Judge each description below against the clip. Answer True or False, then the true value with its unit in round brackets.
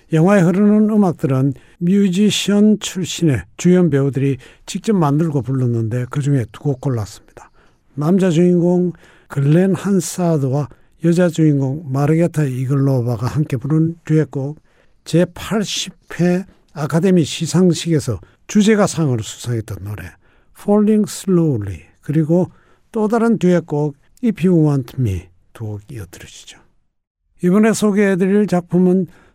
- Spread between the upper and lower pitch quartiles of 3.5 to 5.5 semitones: True (5.2 semitones)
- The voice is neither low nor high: True (160 Hz)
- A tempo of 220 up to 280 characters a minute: False (290 characters per minute)